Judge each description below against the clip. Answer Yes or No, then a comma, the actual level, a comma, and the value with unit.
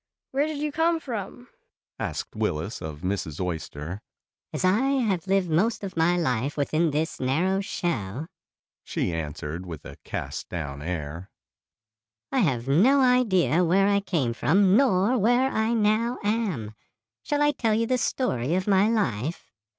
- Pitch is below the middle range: No, medium, 185 Hz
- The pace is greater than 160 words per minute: No, average, 155 wpm